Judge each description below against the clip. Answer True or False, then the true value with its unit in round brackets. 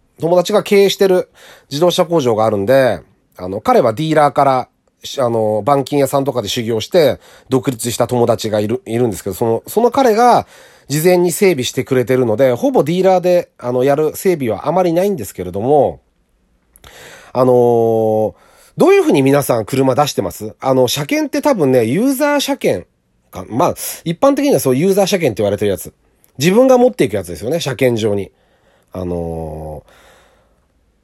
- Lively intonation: True (8.1 semitones)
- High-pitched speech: False (135 Hz)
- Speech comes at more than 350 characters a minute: True (360 characters per minute)